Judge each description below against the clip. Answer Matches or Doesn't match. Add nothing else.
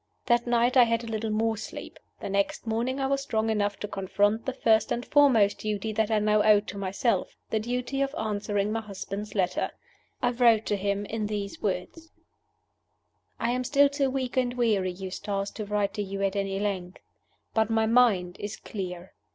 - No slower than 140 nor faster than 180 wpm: Doesn't match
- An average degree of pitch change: Matches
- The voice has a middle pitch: Doesn't match